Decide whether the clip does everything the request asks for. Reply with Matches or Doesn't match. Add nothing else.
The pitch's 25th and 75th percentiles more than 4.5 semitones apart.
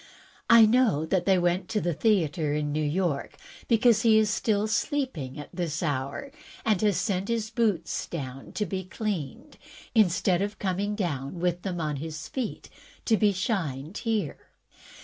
Matches